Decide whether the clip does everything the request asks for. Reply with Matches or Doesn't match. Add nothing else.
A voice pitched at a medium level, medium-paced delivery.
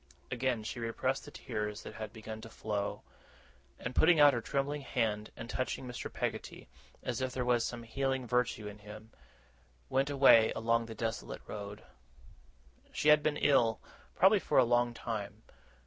Doesn't match